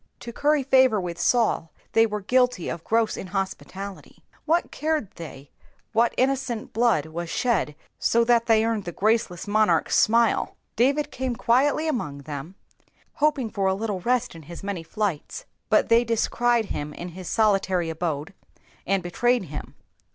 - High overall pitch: Yes, high, 215 Hz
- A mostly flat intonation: No, wide, 5.5 semitones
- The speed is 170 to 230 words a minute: No, average, 155 wpm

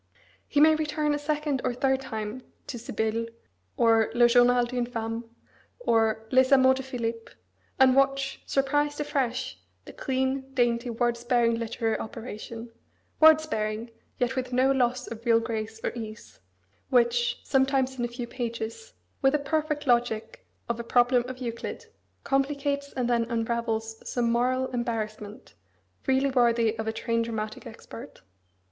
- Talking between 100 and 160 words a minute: Yes, average, 150 wpm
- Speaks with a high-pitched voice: Yes, high, 245 Hz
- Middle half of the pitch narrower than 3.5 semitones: Yes, average, 2.7 semitones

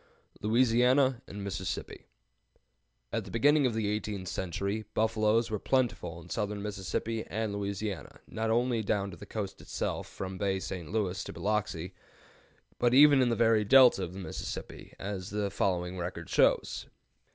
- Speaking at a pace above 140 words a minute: Yes, average, 155 wpm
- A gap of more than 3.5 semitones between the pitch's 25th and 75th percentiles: No, average, 3.0 semitones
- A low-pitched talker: Yes, low, 105 Hz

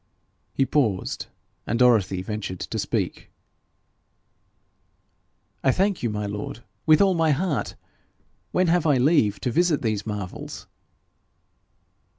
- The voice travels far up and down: Yes, wide, 7.3 semitones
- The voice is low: Yes, low, 125 Hz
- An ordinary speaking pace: No, slow, 120 wpm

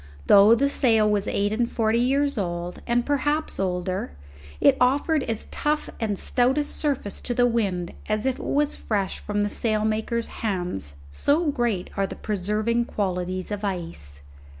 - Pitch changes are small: No, average, 4.4 semitones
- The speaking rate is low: No, average, 165 wpm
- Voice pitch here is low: No, high, 215 Hz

